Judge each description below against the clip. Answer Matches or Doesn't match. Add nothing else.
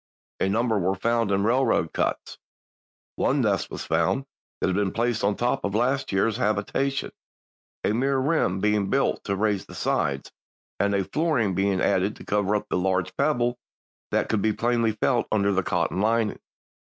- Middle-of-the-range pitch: Doesn't match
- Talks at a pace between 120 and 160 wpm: Doesn't match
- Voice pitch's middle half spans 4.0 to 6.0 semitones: Doesn't match